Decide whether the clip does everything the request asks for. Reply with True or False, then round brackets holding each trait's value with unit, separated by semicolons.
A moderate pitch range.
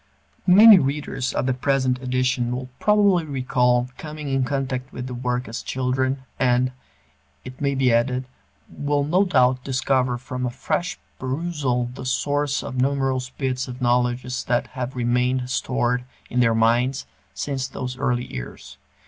False (1.7 semitones)